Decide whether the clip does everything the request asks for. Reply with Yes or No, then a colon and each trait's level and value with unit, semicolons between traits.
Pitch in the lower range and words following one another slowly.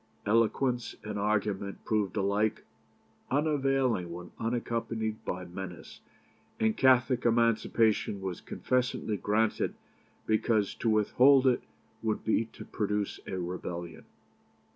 Yes: low, 110 Hz; slow, 105 wpm